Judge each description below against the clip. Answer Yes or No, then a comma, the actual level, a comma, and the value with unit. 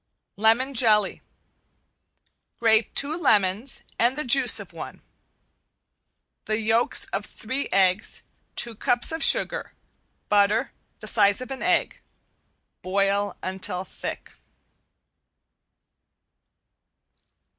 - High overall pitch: Yes, high, 220 Hz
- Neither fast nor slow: No, slow, 95 wpm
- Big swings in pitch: No, average, 4.4 semitones